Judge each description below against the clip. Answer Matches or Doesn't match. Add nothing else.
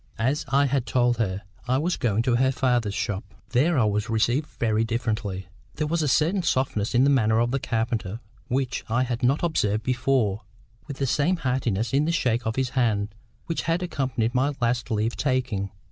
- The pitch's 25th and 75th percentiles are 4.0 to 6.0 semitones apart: Doesn't match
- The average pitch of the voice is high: Doesn't match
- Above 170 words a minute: Matches